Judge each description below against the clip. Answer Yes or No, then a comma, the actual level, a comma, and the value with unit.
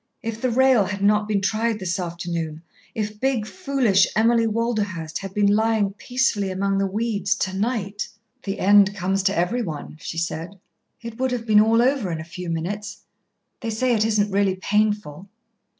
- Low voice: No, high, 205 Hz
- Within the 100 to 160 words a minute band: No, average, 175 wpm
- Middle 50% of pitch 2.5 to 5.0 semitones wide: Yes, average, 3.0 semitones